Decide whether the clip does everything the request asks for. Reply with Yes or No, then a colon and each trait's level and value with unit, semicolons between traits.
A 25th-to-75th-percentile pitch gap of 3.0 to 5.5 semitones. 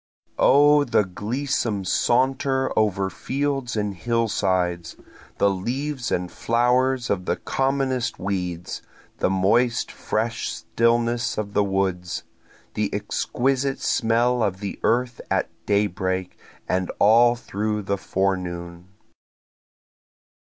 Yes: average, 4.6 semitones